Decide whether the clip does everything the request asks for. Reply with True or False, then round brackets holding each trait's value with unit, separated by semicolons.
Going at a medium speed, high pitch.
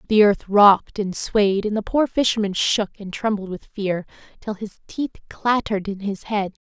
True (190 wpm; 205 Hz)